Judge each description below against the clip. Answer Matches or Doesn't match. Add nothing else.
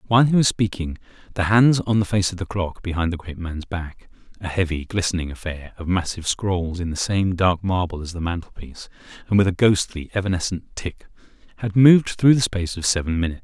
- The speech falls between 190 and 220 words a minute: Matches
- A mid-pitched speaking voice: Doesn't match